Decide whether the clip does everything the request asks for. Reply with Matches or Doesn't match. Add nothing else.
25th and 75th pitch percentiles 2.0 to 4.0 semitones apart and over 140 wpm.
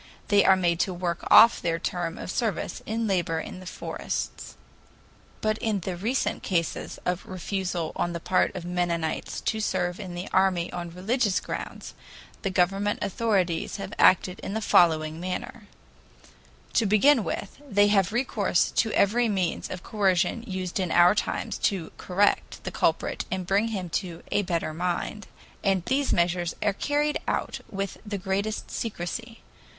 Matches